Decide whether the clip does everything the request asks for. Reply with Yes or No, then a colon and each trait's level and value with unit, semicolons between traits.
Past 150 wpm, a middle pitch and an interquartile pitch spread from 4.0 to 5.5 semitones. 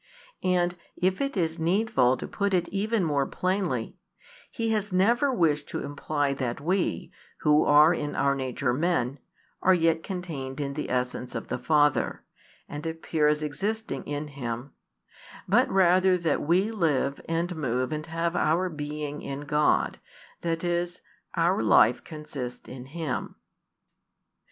No: average, 145 wpm; medium, 155 Hz; average, 4.3 semitones